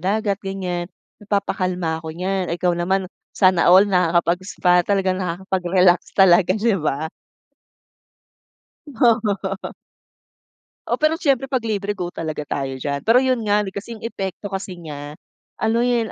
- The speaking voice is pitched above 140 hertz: Yes, high, 190 Hz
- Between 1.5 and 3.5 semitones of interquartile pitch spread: Yes, average, 3.1 semitones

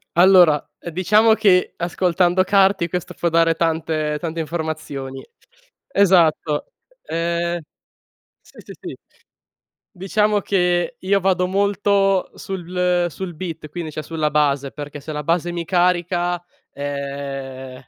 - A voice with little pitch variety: No, average, 3.2 semitones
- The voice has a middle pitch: Yes, medium, 175 Hz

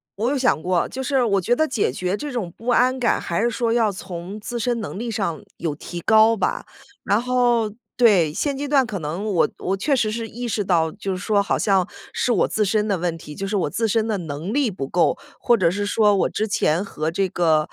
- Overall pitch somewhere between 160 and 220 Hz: Yes, high, 210 Hz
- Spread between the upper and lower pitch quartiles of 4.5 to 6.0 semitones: Yes, average, 4.8 semitones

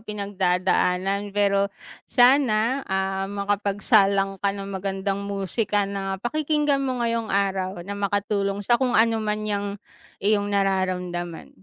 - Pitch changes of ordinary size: No, narrow, 1.7 semitones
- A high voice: Yes, high, 200 Hz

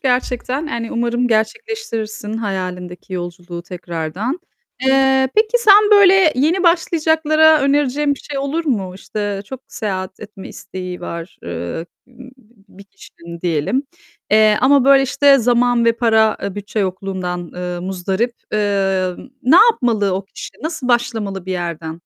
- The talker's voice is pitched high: Yes, high, 225 Hz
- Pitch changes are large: Yes, wide, 6.7 semitones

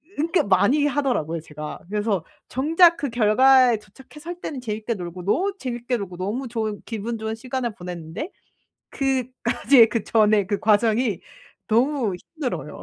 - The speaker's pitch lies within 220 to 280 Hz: Yes, high, 230 Hz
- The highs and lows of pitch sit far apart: No, average, 4.4 semitones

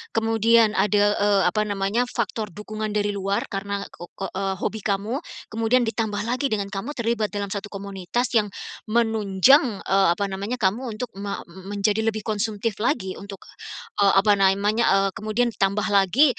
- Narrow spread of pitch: Yes, narrow, 2.2 semitones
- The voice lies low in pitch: No, high, 210 Hz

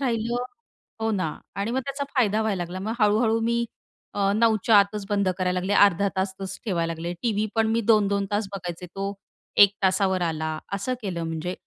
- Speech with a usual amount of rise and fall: Yes, average, 3.2 semitones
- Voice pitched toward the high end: Yes, high, 200 Hz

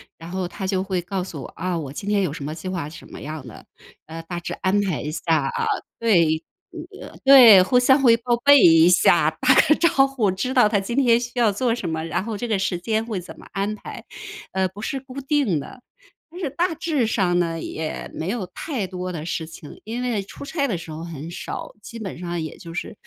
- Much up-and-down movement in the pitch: Yes, wide, 6.1 semitones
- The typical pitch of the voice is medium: No, high, 195 Hz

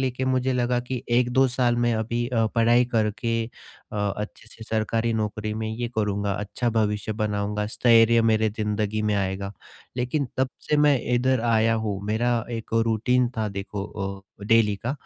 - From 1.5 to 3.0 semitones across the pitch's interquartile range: Yes, narrow, 2.4 semitones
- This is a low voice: Yes, low, 115 Hz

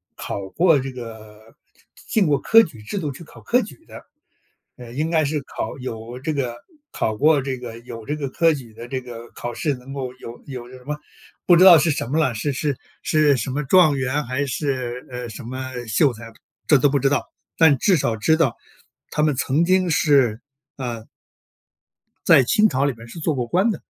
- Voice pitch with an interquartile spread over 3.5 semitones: Yes, average, 4.1 semitones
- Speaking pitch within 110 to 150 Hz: Yes, low, 135 Hz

